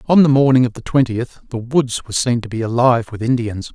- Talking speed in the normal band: No, fast, 240 wpm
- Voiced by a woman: No, male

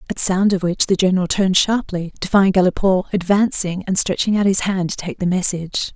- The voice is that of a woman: Yes, female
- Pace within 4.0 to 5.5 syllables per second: No, 5.9 syllables/s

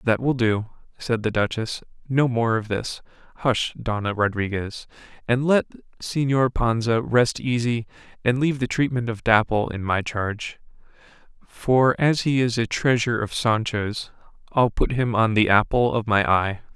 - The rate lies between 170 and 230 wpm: No, average, 160 wpm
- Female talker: No, male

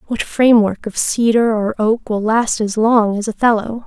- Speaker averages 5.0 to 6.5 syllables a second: No, 4.7 syllables/s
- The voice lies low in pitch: No, high, 220 Hz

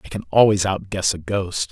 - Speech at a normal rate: No, fast, 210 wpm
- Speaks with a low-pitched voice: Yes, very low, 95 Hz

